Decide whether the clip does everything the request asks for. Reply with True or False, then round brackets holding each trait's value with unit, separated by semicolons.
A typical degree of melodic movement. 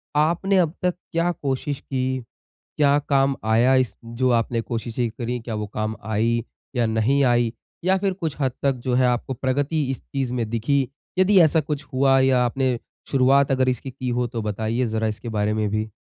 True (3.4 semitones)